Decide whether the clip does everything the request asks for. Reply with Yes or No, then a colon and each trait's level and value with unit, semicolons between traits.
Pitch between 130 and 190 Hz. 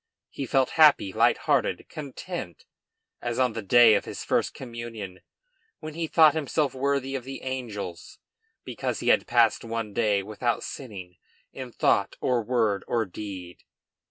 No: low, 120 Hz